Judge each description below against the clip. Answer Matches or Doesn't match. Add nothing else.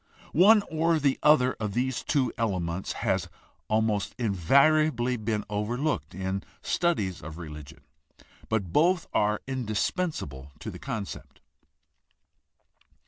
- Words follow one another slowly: Matches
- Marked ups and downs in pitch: Matches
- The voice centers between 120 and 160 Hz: Doesn't match